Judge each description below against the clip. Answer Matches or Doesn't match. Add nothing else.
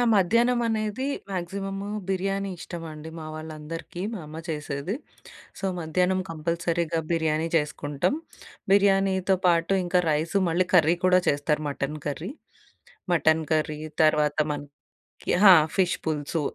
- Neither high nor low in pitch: Matches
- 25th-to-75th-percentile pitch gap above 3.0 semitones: Matches